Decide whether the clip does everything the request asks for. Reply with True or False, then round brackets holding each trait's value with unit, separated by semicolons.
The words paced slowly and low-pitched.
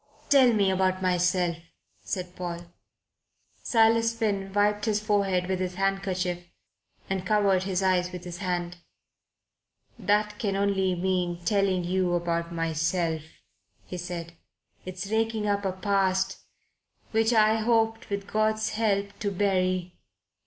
False (130 wpm; 190 Hz)